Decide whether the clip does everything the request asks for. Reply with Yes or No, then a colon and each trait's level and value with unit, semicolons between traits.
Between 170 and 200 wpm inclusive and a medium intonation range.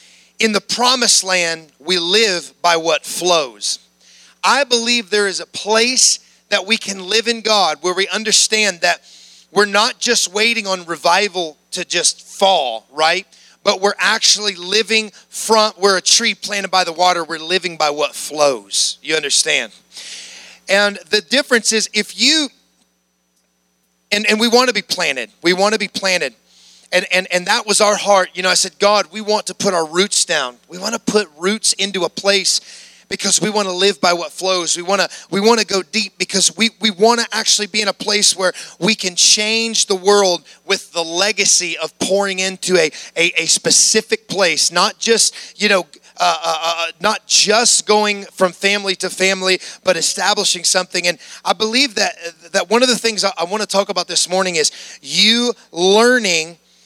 Yes: average, 190 wpm; average, 3.3 semitones